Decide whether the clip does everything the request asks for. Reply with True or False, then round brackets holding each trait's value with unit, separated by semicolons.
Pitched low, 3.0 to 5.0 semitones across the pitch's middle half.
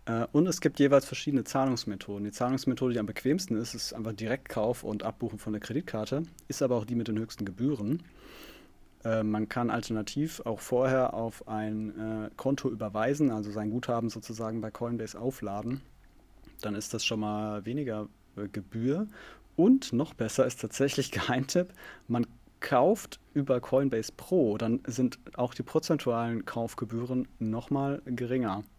True (120 Hz; 3.5 semitones)